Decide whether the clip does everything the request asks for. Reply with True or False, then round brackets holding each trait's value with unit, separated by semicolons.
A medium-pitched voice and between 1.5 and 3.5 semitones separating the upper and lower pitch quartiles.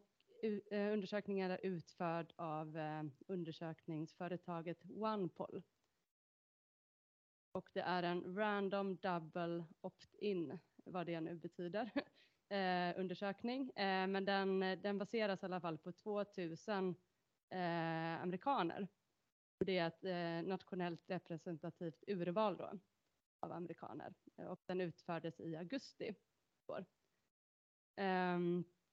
True (180 Hz; 2.7 semitones)